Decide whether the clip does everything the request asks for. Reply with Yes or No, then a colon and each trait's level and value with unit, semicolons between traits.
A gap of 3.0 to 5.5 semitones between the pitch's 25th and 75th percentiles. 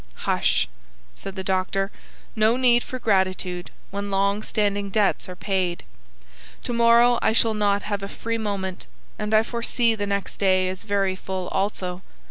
No: narrow, 2.5 semitones